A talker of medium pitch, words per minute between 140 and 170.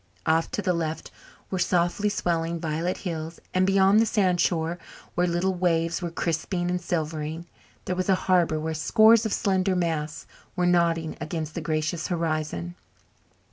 Yes: medium, 170 Hz; average, 155 wpm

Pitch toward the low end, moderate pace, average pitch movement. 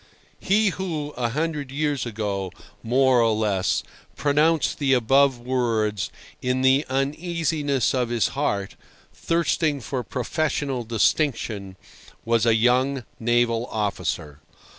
No: low, 130 Hz; slow, 115 wpm; average, 4.3 semitones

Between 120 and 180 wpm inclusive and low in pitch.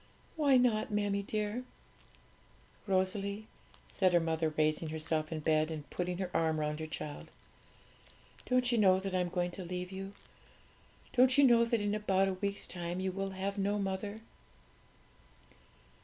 No: average, 160 wpm; high, 190 Hz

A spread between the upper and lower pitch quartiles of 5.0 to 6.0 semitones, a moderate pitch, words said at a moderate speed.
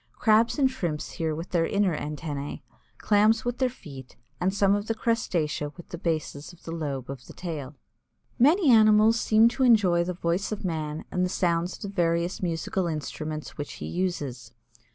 Yes: wide, 5.5 semitones; medium, 175 Hz; average, 185 wpm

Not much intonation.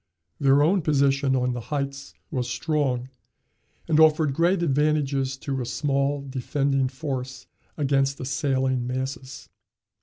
Yes: narrow, 2.0 semitones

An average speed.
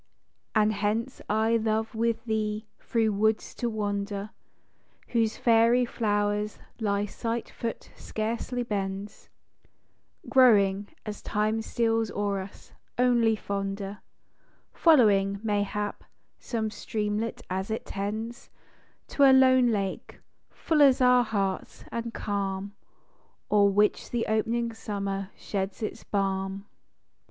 No: slow, 115 wpm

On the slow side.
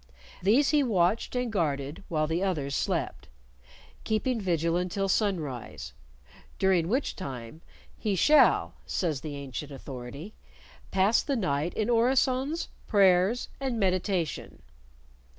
Yes: slow, 115 wpm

